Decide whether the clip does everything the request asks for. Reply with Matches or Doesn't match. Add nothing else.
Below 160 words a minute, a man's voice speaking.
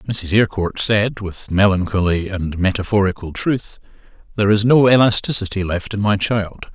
Matches